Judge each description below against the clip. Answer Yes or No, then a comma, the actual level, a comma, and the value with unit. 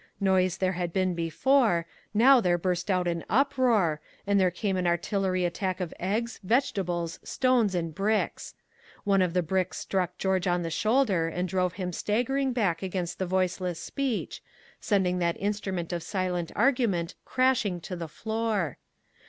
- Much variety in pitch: No, average, 3.3 semitones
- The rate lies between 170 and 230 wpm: No, average, 160 wpm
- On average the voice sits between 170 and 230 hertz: Yes, medium, 185 Hz